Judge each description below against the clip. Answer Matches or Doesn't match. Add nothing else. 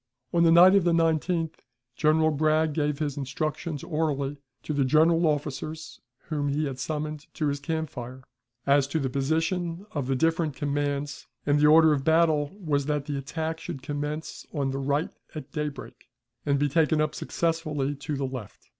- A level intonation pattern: Matches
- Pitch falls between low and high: Matches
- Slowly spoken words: Doesn't match